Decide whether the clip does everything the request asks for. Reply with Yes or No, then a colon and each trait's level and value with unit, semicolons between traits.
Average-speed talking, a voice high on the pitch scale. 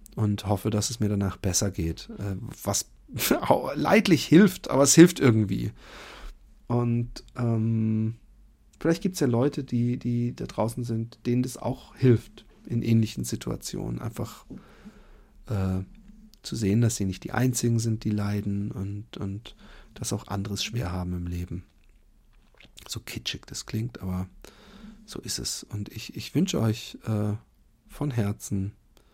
No: average, 145 wpm; low, 110 Hz